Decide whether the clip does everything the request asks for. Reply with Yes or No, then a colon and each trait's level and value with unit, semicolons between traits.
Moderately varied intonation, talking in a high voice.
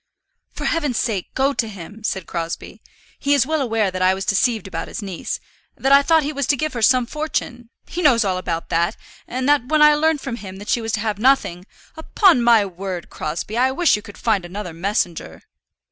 No: wide, 6.5 semitones; high, 225 Hz